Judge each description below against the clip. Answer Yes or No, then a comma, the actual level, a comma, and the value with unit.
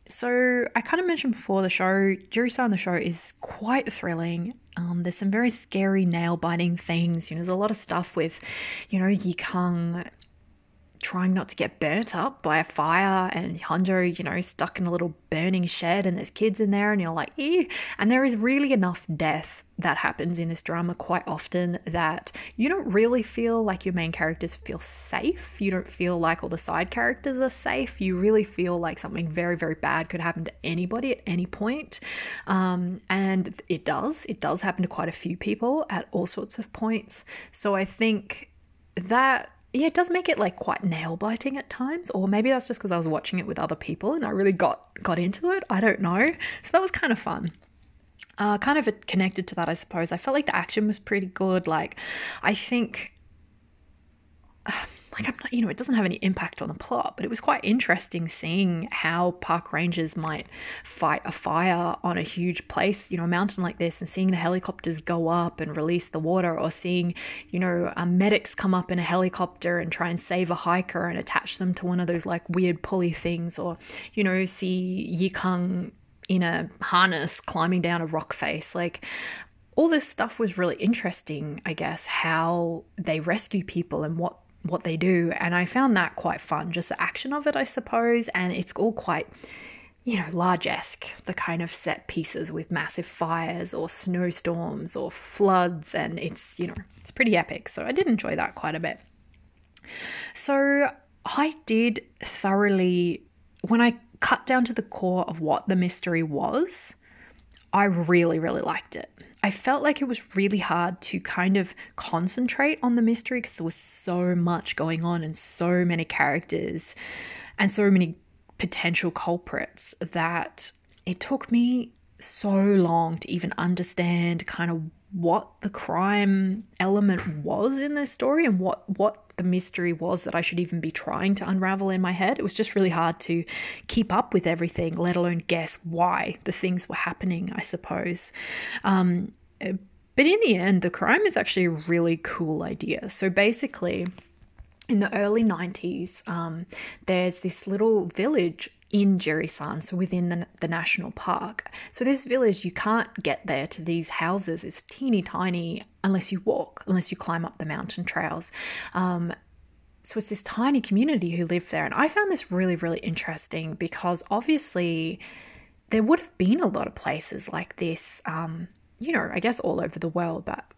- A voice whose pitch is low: No, medium, 180 Hz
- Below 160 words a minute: No, average, 190 wpm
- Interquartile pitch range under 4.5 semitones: Yes, average, 3.8 semitones